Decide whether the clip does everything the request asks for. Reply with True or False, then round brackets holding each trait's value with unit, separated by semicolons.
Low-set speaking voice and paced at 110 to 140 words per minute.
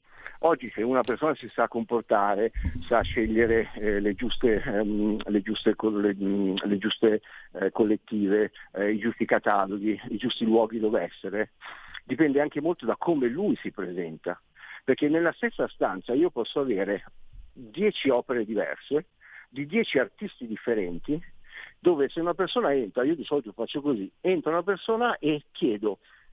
False (115 Hz; 155 wpm)